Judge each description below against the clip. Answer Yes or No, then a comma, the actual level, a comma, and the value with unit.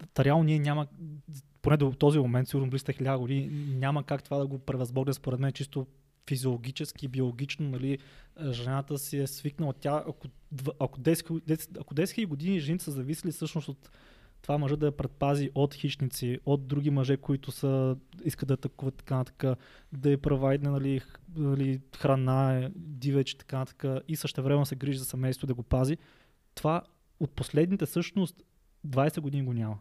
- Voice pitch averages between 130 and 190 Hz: Yes, medium, 140 Hz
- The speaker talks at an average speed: No, fast, 175 wpm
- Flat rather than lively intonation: Yes, narrow, 1.9 semitones